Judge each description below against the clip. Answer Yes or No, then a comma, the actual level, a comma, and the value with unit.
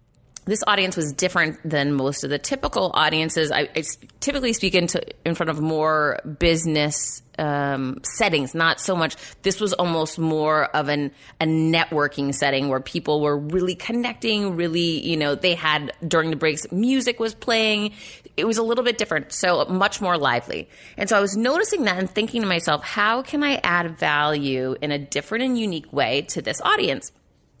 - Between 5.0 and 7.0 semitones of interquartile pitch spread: Yes, wide, 5.6 semitones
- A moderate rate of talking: Yes, average, 185 wpm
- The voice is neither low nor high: Yes, medium, 165 Hz